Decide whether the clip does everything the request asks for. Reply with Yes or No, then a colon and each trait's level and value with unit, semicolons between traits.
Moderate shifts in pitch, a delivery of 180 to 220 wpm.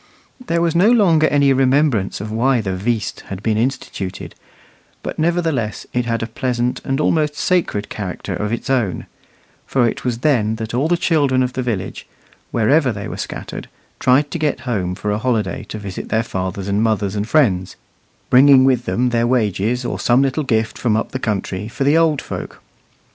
Yes: average, 4.5 semitones; average, 190 wpm